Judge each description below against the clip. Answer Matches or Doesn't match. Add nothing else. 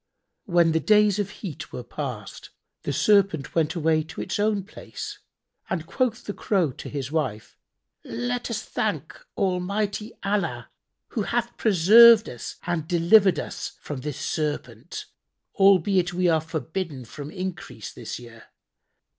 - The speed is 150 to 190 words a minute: Doesn't match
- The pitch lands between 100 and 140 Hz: Doesn't match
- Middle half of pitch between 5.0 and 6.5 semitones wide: Matches